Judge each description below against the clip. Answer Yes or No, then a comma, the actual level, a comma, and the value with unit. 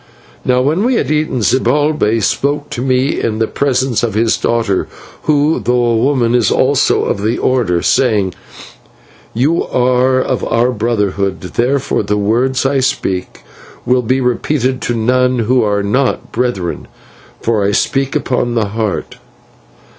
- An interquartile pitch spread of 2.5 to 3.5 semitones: Yes, average, 3.1 semitones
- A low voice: Yes, low, 125 Hz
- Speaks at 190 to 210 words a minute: No, average, 150 wpm